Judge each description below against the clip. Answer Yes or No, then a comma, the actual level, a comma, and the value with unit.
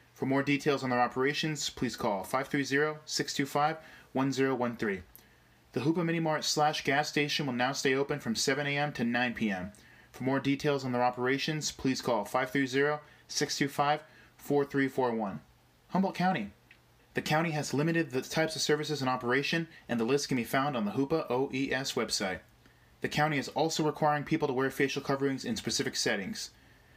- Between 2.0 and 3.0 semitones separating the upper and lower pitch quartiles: Yes, average, 2.7 semitones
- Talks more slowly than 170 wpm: Yes, average, 160 wpm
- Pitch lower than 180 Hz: Yes, medium, 140 Hz